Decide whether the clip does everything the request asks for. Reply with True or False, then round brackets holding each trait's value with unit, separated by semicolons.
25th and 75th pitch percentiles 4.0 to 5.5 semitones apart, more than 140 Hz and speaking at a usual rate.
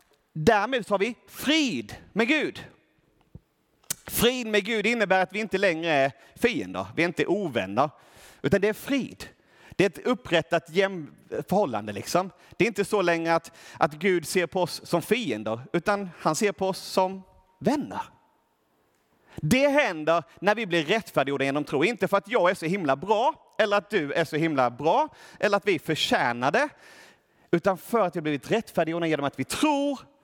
True (4.6 semitones; 190 Hz; 175 wpm)